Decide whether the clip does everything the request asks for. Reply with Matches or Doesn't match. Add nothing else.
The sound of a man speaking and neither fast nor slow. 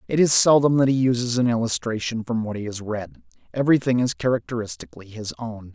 Matches